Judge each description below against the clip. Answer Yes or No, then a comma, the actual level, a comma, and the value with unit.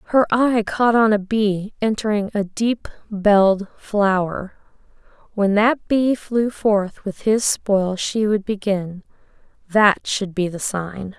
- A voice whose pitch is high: Yes, high, 205 Hz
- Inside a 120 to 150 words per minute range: Yes, average, 140 wpm